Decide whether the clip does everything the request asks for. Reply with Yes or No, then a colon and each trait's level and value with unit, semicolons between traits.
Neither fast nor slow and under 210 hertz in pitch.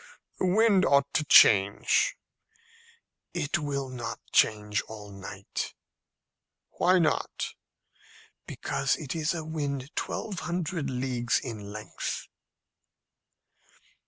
No: slow, 100 wpm; medium, 140 Hz